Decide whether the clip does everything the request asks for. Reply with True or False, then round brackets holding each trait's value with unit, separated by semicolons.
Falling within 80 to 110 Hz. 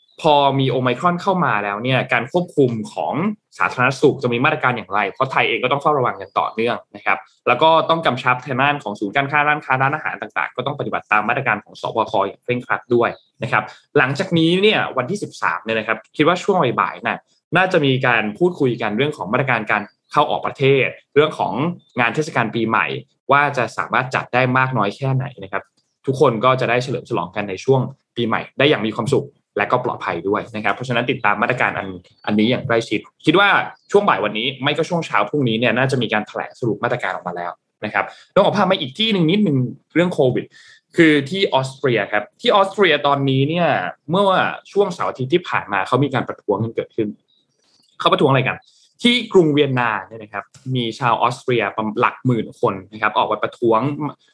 False (130 Hz)